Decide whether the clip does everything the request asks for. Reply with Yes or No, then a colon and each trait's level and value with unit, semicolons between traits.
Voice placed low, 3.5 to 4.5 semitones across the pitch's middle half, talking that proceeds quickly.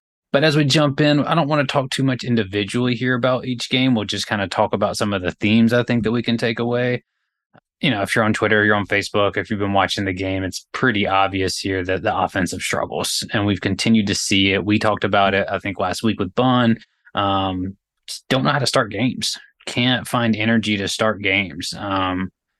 Yes: low, 105 Hz; average, 3.8 semitones; fast, 230 wpm